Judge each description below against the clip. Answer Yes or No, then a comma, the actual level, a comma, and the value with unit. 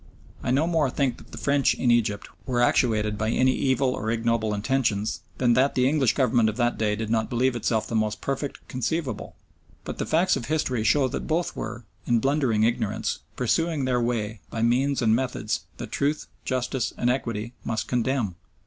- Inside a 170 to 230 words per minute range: Yes, average, 190 wpm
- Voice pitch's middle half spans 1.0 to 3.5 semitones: Yes, average, 3.2 semitones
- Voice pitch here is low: Yes, low, 125 Hz